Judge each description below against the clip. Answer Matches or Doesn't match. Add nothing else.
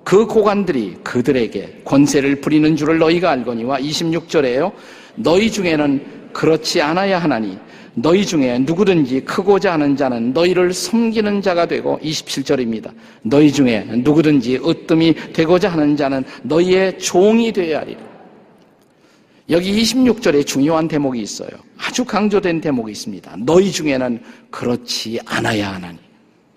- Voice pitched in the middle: Matches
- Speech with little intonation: Doesn't match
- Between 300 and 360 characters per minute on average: Matches